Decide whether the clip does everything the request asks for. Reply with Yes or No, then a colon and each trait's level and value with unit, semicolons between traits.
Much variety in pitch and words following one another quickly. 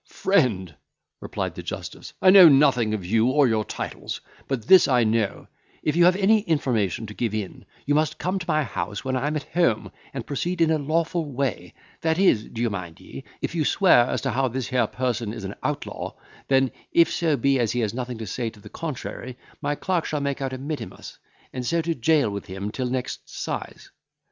Yes: wide, 5.7 semitones; fast, 210 wpm